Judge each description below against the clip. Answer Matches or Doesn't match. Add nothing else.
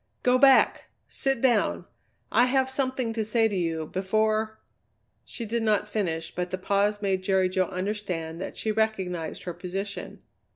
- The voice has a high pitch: Matches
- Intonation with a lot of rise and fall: Doesn't match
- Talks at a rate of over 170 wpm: Doesn't match